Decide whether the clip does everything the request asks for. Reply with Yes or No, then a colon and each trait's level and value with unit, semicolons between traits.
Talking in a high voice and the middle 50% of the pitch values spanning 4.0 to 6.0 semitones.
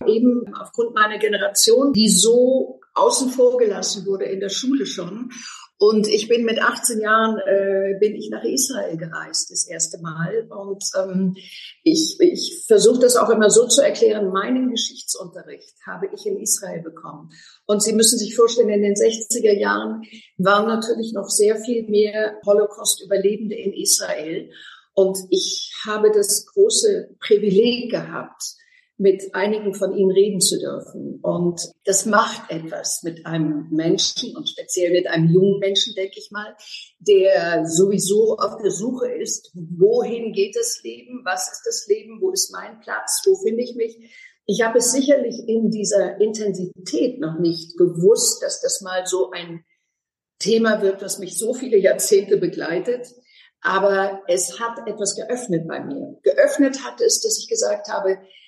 Yes: high, 215 Hz; average, 4.4 semitones